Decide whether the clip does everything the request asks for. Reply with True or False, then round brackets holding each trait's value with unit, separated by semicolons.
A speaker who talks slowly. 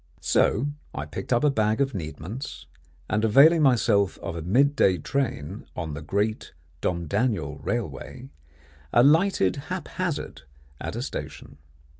True (130 wpm)